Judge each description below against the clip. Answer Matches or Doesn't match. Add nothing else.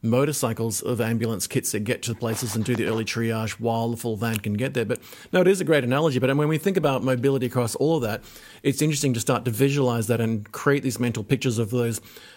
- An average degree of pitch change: Matches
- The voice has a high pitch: Doesn't match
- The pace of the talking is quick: Matches